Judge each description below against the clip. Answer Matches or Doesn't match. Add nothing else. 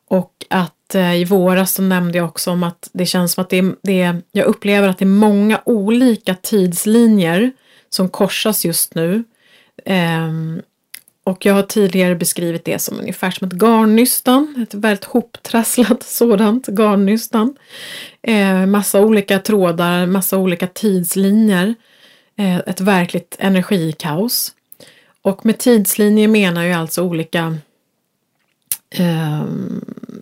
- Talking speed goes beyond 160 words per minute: Doesn't match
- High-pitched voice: Matches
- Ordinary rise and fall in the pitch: Matches